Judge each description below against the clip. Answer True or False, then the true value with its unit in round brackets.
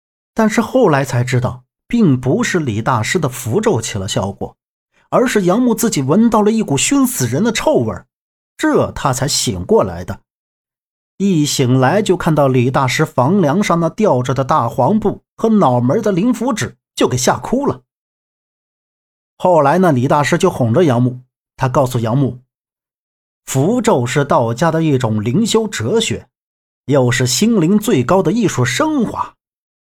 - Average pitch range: False (8.8 semitones)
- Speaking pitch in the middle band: True (150 Hz)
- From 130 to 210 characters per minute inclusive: False (230 characters per minute)